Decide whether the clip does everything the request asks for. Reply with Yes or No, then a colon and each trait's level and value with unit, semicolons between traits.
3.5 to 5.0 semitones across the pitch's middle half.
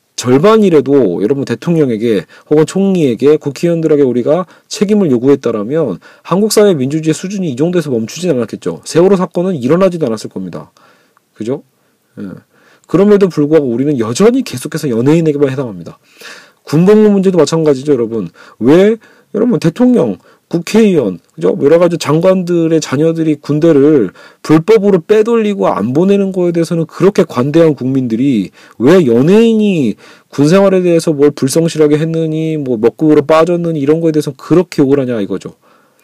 Yes: average, 4.6 semitones